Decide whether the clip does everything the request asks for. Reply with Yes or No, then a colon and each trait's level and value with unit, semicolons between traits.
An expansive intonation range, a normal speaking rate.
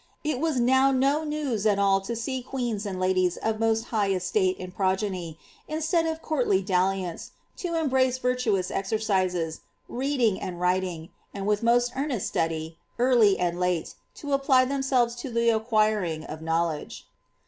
Yes: wide, 5.8 semitones; average, 160 wpm